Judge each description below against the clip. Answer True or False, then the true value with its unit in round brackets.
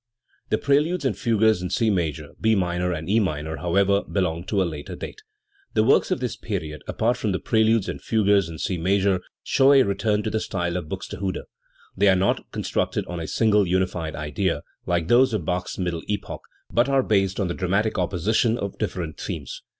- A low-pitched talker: True (95 Hz)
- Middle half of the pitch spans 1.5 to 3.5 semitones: False (3.9 semitones)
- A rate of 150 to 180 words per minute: False (200 wpm)